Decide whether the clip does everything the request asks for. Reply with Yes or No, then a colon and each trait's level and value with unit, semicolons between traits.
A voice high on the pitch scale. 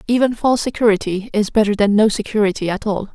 Yes: high, 210 Hz